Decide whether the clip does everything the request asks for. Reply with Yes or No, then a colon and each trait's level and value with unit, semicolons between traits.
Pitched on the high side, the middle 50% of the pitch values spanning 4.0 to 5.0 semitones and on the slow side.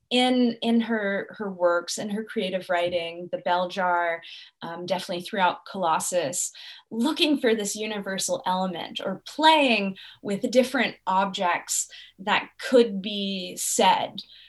Yes: high, 195 Hz; average, 4.4 semitones; slow, 125 wpm